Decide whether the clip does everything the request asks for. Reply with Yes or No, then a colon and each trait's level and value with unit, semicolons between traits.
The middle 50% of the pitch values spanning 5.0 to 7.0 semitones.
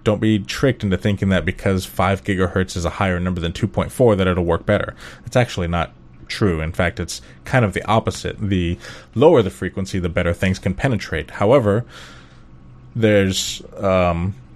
No: average, 3.3 semitones